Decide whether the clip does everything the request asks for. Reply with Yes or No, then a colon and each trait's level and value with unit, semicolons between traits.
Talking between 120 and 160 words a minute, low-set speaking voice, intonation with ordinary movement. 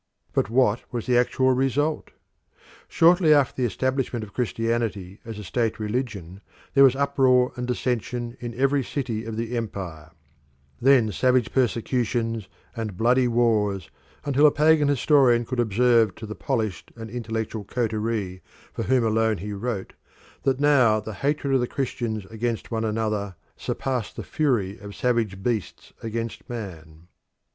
Yes: average, 150 wpm; low, 115 Hz; average, 3.1 semitones